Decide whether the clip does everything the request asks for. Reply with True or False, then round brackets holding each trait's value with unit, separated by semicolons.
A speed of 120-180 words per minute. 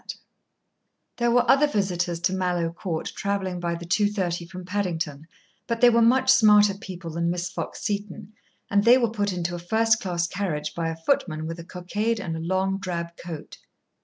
False (190 wpm)